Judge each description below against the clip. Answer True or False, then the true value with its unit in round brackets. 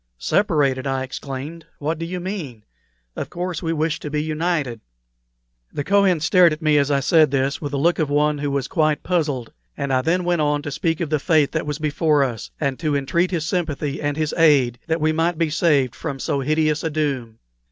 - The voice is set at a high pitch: False (150 Hz)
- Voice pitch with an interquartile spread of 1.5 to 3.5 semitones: True (2.8 semitones)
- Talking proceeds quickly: True (215 wpm)